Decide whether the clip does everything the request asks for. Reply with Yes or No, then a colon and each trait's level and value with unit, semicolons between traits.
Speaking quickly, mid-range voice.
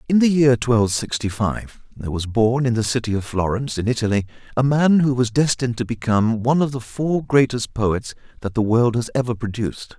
No: fast, 210 wpm; low, 120 Hz